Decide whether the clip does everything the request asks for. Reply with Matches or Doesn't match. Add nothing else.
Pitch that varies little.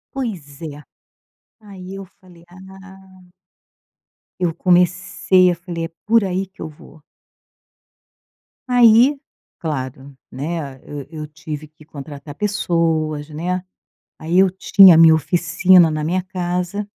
Doesn't match